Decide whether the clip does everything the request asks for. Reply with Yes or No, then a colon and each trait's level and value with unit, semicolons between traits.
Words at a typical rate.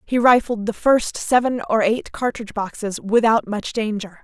Yes: average, 170 wpm